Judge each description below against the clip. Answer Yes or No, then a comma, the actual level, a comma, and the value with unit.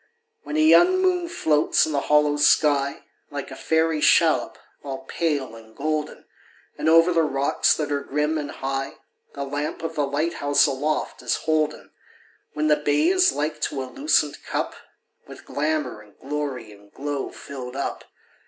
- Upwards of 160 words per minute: Yes, average, 170 wpm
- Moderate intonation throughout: No, narrow, 2.2 semitones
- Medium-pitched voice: Yes, medium, 150 Hz